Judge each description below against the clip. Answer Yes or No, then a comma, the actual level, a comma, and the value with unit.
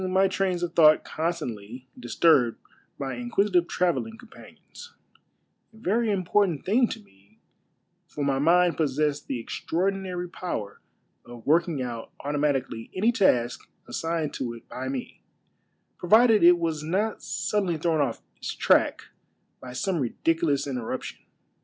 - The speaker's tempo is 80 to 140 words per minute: Yes, slow, 135 wpm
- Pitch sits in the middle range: Yes, medium, 165 Hz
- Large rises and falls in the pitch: Yes, wide, 5.9 semitones